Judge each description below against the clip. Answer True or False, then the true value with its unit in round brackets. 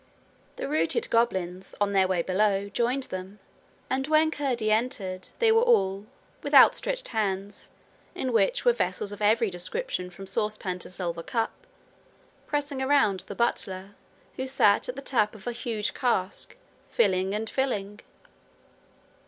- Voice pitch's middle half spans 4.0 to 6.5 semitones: True (5.5 semitones)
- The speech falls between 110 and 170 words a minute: True (150 wpm)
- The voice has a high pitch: True (215 Hz)